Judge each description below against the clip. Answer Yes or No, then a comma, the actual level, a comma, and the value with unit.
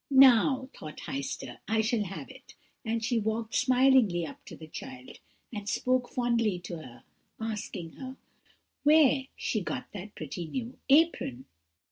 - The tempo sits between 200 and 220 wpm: No, average, 145 wpm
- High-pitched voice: Yes, high, 225 Hz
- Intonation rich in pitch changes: Yes, wide, 6.2 semitones